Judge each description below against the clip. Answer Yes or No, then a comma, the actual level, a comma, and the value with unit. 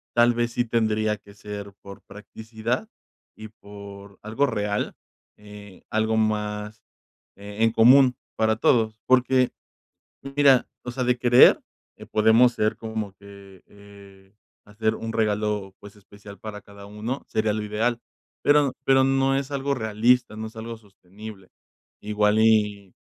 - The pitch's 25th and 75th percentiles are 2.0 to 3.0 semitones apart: Yes, narrow, 2.4 semitones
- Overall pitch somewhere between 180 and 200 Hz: No, low, 110 Hz